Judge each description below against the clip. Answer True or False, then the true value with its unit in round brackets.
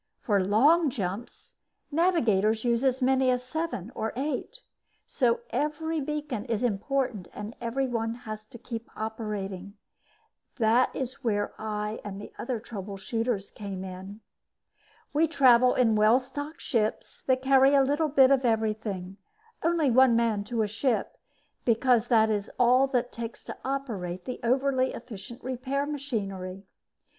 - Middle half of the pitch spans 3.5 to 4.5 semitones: True (3.9 semitones)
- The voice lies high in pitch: True (235 Hz)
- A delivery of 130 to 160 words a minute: True (145 wpm)